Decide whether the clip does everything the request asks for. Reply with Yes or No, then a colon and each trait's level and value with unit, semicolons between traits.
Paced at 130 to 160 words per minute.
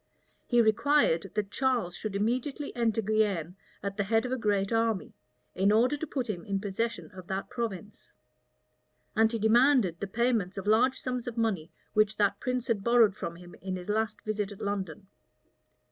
No: average, 180 wpm